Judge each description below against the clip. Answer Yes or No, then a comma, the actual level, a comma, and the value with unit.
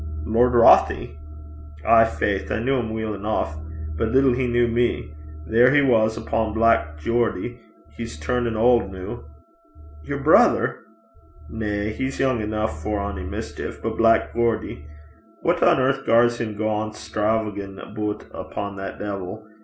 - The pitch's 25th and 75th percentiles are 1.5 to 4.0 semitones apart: Yes, narrow, 2.6 semitones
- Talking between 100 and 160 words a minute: Yes, average, 145 wpm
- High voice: No, low, 110 Hz